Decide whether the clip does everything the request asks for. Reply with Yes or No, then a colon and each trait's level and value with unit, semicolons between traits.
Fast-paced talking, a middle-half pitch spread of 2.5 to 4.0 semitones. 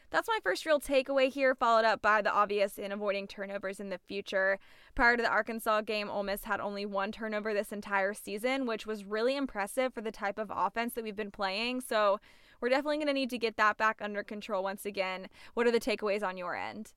Yes: fast, 225 wpm; average, 2.9 semitones